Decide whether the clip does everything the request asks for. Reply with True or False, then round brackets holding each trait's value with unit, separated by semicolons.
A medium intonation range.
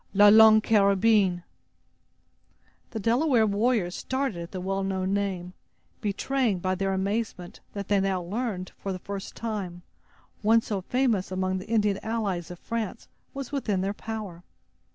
True (3.0 semitones)